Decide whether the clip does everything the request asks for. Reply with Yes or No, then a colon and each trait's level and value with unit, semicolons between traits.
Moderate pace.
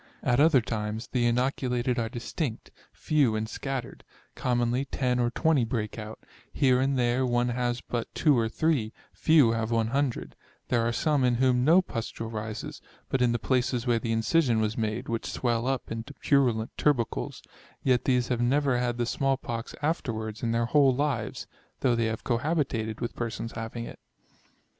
Yes: average, 175 wpm